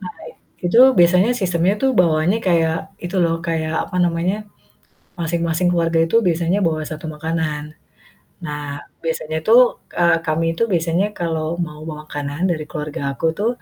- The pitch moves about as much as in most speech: No, narrow, 1.9 semitones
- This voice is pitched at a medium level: Yes, medium, 165 Hz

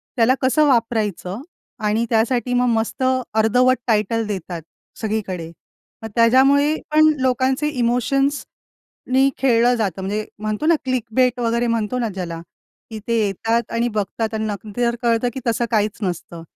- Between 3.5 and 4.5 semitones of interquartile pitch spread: No, average, 2.9 semitones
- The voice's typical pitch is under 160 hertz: No, high, 230 Hz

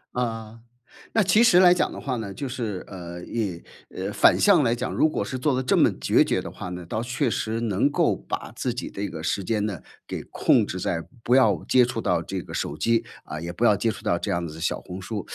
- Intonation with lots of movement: Yes, wide, 5.7 semitones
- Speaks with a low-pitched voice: Yes, low, 110 Hz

